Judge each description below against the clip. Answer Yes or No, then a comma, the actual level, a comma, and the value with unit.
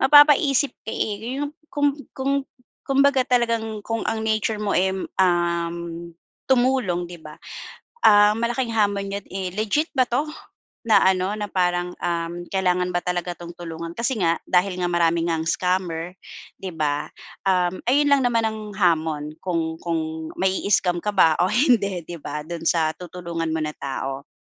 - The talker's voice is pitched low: No, medium, 185 Hz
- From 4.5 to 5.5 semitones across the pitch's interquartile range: Yes, average, 4.8 semitones